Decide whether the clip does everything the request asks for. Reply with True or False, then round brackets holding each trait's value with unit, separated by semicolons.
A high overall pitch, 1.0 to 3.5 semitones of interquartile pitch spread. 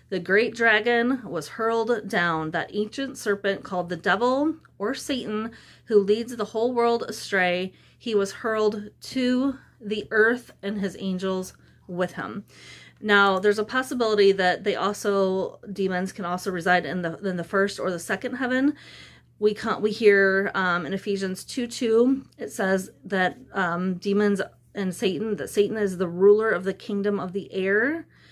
True (205 Hz; 2.9 semitones)